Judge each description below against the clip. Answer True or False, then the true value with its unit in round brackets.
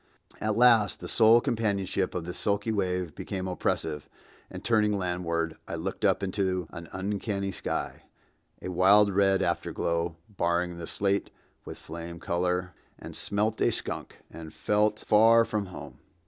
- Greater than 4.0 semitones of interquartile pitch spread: False (3.2 semitones)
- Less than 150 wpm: True (140 wpm)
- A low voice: True (95 Hz)